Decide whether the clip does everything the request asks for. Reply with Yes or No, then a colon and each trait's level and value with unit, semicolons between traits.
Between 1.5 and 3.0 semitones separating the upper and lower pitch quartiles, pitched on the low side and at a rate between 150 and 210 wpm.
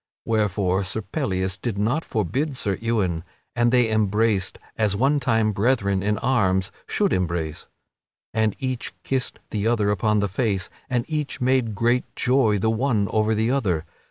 No: average, 3.8 semitones; low, 110 Hz; average, 155 wpm